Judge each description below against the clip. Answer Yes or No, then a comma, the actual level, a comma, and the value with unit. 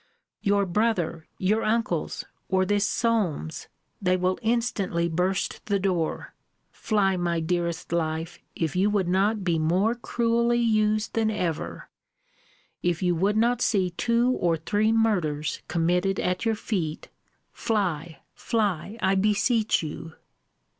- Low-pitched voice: No, high, 190 Hz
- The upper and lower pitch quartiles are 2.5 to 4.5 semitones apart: Yes, average, 4.2 semitones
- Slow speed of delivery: Yes, slow, 130 wpm